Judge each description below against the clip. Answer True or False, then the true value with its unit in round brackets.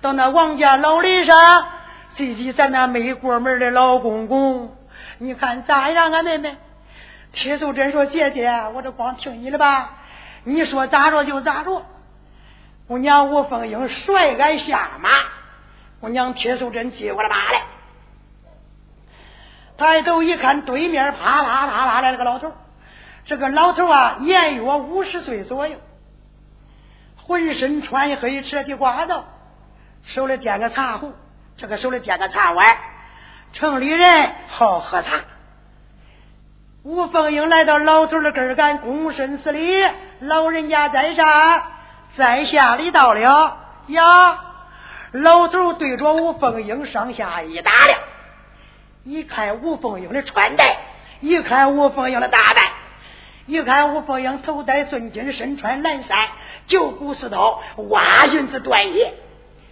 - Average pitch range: True (3.8 semitones)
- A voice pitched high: True (285 Hz)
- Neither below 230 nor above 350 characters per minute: False (200 characters per minute)